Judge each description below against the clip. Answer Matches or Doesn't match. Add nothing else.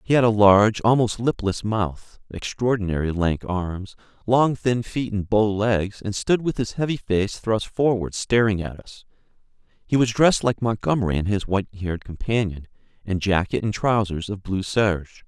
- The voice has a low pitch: Matches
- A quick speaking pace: Doesn't match